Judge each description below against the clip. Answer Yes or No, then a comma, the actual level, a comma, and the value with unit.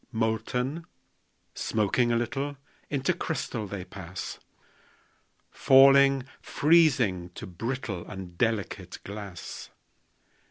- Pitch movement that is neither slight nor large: No, wide, 5.7 semitones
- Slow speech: Yes, slow, 85 wpm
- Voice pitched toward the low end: Yes, low, 115 Hz